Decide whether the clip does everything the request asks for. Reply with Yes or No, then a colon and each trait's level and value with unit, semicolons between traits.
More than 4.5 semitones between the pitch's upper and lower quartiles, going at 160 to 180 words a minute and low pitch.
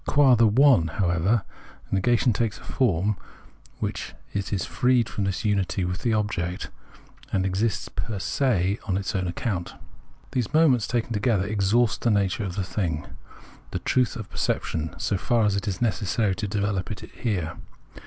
No: average, 3.7 semitones; average, 175 wpm; low, 100 Hz